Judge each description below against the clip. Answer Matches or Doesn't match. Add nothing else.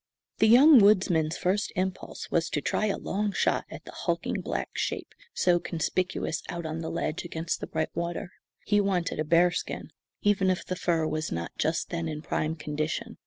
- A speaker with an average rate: Matches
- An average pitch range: Matches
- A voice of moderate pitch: Matches